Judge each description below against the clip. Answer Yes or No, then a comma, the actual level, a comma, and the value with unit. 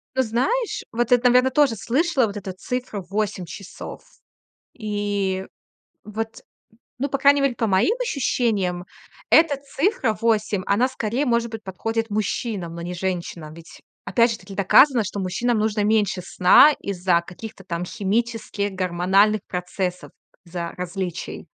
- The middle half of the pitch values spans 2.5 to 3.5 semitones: No, average, 4.4 semitones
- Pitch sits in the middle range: No, high, 210 Hz